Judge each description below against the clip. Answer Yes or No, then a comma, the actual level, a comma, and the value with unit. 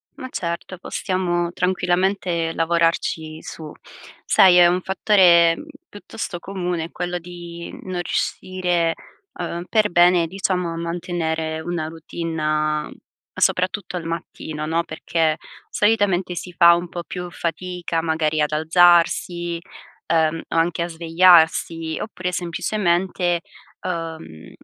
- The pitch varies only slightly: Yes, narrow, 1.7 semitones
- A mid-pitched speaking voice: Yes, medium, 175 Hz